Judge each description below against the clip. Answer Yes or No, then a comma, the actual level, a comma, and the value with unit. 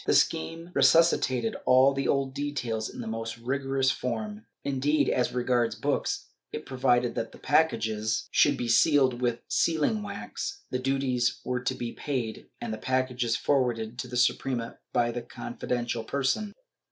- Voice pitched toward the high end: No, low, 125 Hz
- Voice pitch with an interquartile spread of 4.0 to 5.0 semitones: No, narrow, 2.6 semitones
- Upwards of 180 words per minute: No, average, 155 wpm